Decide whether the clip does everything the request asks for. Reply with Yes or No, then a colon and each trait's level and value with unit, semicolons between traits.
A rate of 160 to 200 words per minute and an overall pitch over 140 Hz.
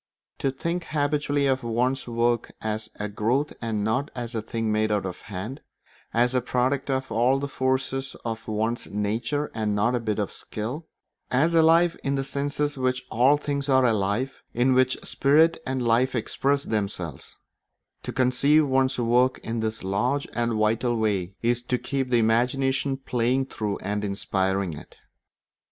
No: average, 170 wpm; low, 125 Hz